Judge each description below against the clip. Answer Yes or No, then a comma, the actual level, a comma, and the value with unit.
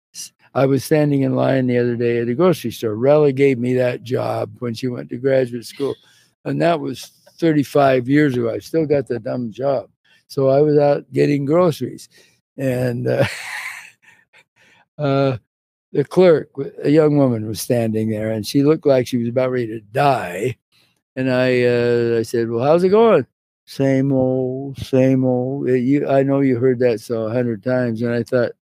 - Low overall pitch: Yes, low, 130 Hz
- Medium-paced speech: Yes, average, 185 wpm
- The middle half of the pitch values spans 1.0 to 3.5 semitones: Yes, narrow, 2.5 semitones